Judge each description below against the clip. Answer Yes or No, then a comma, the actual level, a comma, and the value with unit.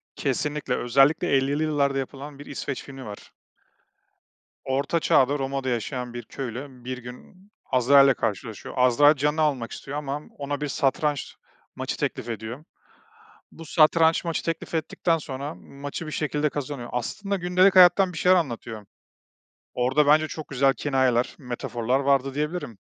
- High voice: No, medium, 140 Hz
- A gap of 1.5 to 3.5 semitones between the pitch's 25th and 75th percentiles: Yes, average, 3.0 semitones